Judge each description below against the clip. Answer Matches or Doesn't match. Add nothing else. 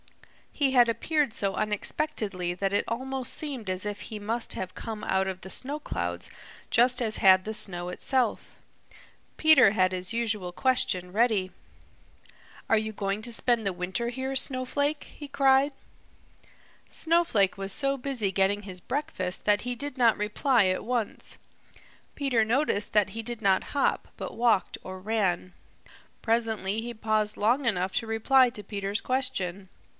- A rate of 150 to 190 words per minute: Matches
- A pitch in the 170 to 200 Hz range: Doesn't match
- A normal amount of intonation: Matches